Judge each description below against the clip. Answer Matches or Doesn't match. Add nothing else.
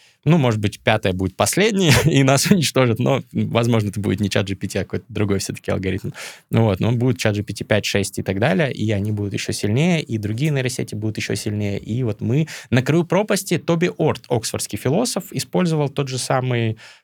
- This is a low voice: Matches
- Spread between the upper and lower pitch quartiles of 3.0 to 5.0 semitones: Doesn't match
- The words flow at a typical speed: Doesn't match